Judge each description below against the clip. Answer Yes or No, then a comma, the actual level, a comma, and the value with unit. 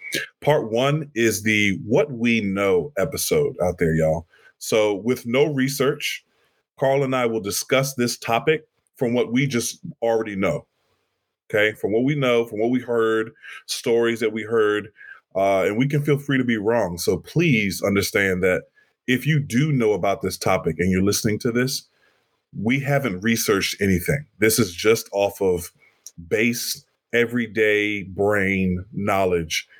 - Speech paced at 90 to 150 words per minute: No, average, 160 wpm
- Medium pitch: No, low, 115 Hz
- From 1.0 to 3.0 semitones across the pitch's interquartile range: No, average, 3.8 semitones